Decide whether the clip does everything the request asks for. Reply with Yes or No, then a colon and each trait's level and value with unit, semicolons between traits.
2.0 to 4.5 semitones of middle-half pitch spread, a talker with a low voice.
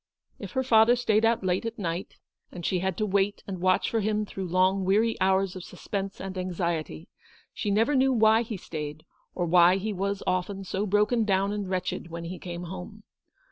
No: average, 2.8 semitones; high, 195 Hz